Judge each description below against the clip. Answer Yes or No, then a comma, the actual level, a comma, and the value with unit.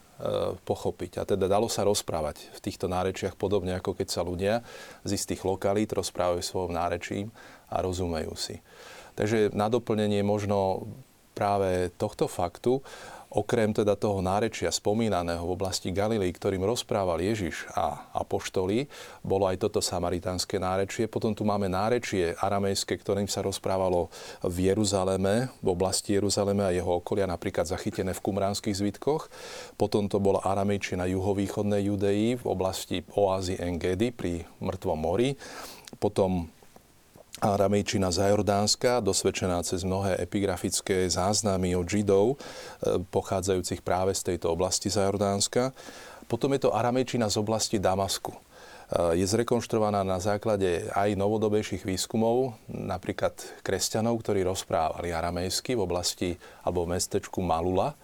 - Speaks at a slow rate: No, average, 130 wpm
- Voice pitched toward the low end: Yes, low, 100 Hz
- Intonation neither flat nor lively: No, narrow, 2.2 semitones